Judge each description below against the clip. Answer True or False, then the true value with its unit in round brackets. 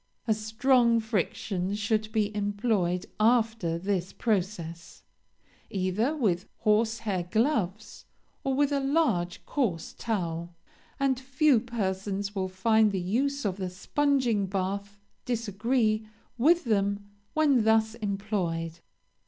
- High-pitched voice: True (215 Hz)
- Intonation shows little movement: False (3.8 semitones)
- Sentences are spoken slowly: True (110 wpm)